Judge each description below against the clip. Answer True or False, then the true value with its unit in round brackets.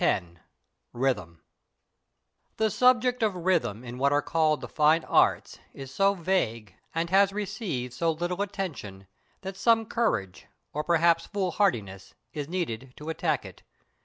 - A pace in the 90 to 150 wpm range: True (140 wpm)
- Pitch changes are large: True (7.4 semitones)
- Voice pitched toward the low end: False (165 Hz)